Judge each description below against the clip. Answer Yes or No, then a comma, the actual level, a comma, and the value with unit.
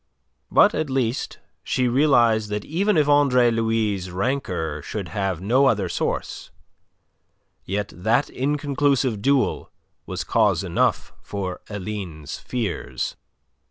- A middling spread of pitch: No, wide, 5.7 semitones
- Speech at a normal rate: No, slow, 115 wpm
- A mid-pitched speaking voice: No, low, 115 Hz